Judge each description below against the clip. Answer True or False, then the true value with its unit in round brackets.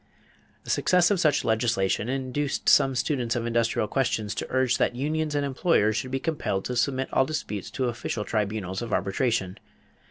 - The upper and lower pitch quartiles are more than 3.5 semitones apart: True (4.2 semitones)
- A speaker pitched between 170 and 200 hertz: False (125 Hz)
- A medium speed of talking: True (170 wpm)